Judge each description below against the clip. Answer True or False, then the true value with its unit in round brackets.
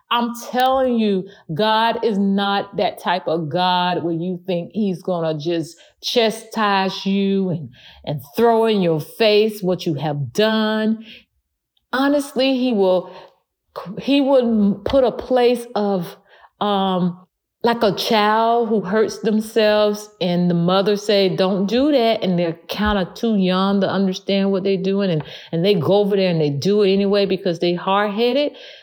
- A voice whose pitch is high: True (200 Hz)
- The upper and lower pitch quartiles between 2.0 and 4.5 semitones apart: True (3.3 semitones)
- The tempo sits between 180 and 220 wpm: False (160 wpm)